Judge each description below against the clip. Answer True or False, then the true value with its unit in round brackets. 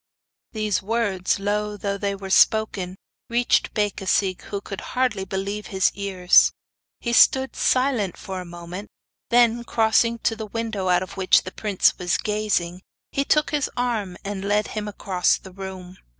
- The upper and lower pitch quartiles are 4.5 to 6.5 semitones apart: False (2.8 semitones)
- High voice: True (205 Hz)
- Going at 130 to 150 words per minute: False (160 wpm)